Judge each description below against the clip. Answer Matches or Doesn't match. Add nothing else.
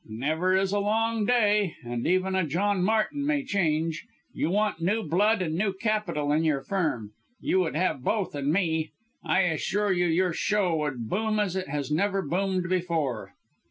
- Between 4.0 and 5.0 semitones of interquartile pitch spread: Matches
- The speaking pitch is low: Doesn't match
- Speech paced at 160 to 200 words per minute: Matches